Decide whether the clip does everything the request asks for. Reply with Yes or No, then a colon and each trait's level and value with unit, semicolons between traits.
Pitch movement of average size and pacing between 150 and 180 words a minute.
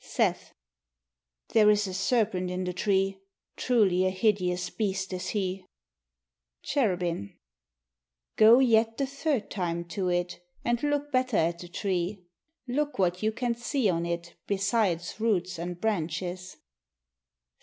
No: average, 4.0 semitones; slow, 135 wpm